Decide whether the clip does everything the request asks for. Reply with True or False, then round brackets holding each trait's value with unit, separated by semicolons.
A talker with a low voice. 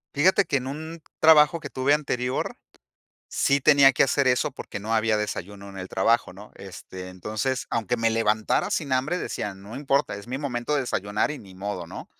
True (120 Hz)